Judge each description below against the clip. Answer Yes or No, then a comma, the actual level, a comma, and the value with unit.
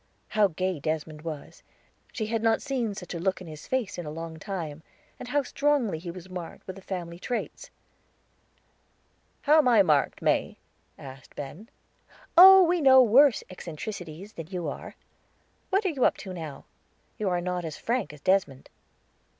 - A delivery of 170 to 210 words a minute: Yes, average, 175 wpm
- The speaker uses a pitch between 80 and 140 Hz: No, medium, 185 Hz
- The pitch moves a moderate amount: No, wide, 6.6 semitones